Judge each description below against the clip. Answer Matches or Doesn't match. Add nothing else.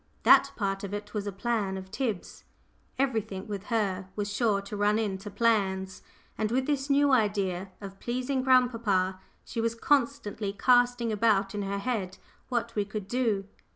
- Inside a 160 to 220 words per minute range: Matches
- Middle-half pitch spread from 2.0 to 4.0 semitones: Matches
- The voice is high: Matches